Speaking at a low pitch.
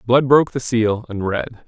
Yes: low, 115 Hz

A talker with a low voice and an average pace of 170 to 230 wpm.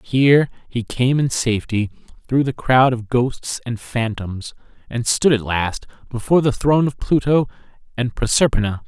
No: low, 125 Hz; average, 155 wpm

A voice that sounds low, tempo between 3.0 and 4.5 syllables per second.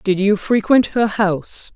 No: high, 205 Hz; 4.2 syllables/s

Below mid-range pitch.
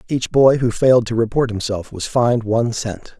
Yes: low, 115 Hz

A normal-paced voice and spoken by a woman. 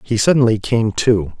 No: average, 170 wpm; male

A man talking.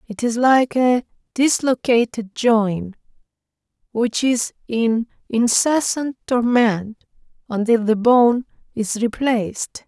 No: female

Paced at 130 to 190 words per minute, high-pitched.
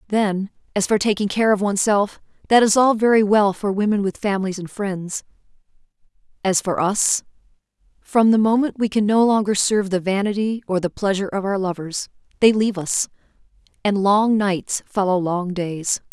Yes: average, 170 wpm; high, 200 Hz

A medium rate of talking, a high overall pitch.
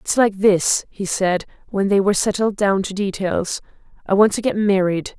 Yes: average, 195 wpm; high, 195 Hz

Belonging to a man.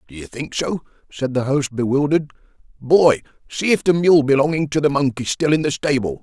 Yes: male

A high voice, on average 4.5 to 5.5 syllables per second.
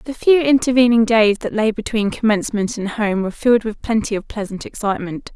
No: high, 220 Hz; 6.0 syllables/s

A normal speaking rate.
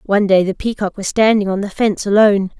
No: fast, 230 wpm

